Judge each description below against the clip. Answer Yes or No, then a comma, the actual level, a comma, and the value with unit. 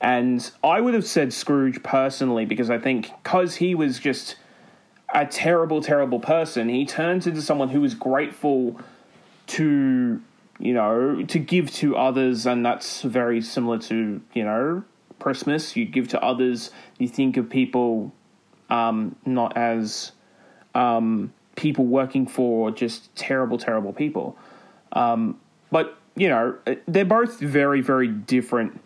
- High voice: No, low, 135 Hz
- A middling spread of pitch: No, wide, 5.8 semitones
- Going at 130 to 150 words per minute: Yes, average, 140 wpm